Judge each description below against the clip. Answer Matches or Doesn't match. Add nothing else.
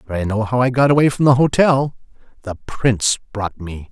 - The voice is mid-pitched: Doesn't match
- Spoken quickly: Matches